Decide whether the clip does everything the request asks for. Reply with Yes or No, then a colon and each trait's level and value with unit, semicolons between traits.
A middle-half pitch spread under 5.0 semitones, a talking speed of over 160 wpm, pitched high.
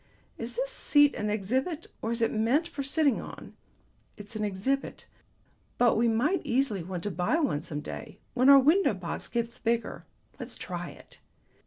No: average, 5.3 semitones; average, 175 wpm; high, 235 Hz